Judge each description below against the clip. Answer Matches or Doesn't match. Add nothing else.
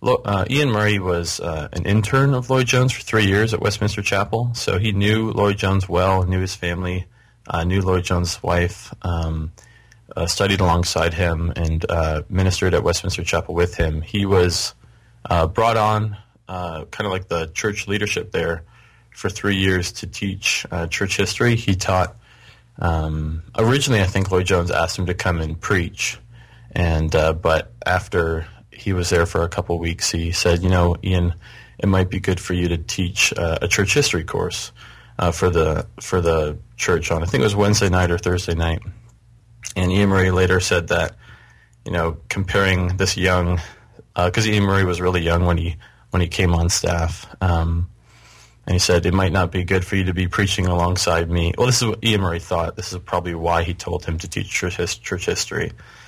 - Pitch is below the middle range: Matches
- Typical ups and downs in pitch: Matches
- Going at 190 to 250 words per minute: Matches